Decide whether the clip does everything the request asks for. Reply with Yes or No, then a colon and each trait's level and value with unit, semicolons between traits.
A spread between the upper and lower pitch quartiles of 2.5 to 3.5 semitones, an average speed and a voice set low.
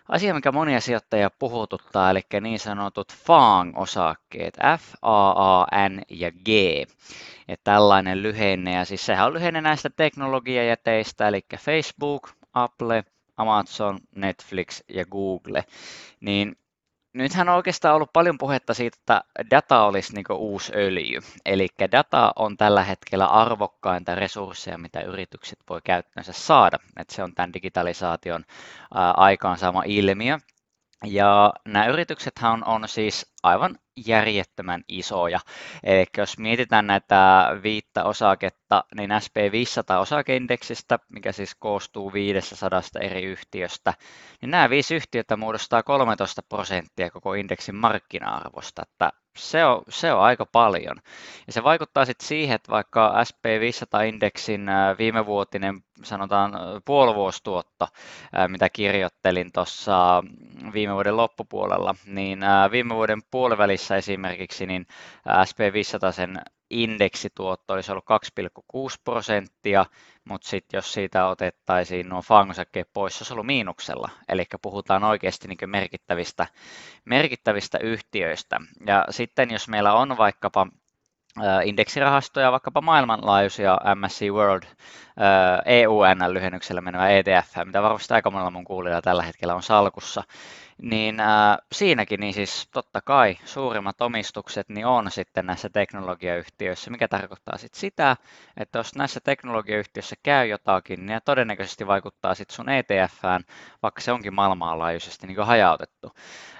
Yes: average, 3.2 semitones; average, 120 wpm; low, 100 Hz